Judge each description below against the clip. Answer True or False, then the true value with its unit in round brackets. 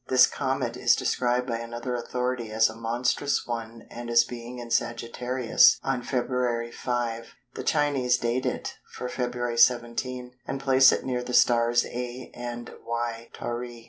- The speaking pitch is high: False (120 Hz)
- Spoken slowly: False (155 wpm)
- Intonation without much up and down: True (1.2 semitones)